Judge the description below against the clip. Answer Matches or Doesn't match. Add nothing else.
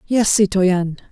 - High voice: Matches